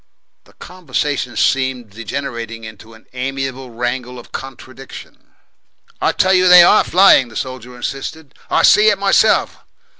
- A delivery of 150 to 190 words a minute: No, average, 140 wpm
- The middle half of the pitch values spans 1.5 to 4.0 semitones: No, average, 4.8 semitones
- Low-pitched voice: Yes, low, 130 Hz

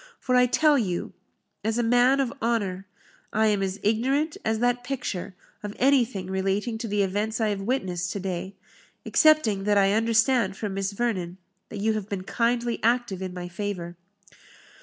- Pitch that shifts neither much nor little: Yes, average, 3.9 semitones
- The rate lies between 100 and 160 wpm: No, average, 175 wpm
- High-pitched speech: Yes, high, 215 Hz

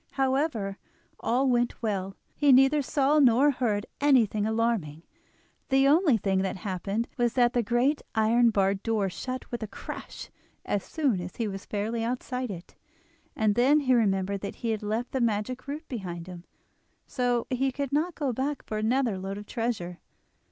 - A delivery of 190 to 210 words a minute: No, average, 170 wpm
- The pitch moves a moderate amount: Yes, average, 4.5 semitones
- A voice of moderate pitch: No, high, 235 Hz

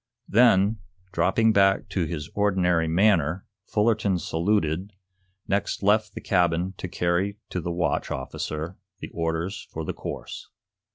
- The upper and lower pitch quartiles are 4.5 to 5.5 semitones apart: No, average, 3.5 semitones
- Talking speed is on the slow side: Yes, slow, 130 wpm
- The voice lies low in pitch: Yes, very low, 90 Hz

